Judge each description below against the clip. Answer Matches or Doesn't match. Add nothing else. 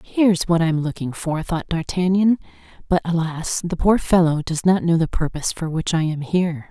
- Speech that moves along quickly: Matches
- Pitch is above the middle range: Doesn't match